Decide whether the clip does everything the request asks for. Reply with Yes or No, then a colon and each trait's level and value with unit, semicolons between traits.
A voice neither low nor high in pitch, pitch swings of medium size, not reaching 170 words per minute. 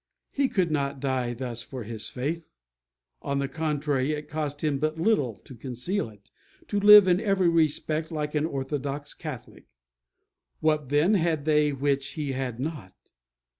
Yes: medium, 145 Hz; average, 3.2 semitones; average, 160 wpm